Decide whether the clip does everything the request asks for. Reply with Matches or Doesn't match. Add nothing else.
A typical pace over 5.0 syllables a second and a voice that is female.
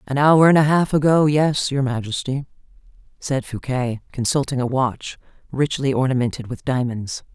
Doesn't match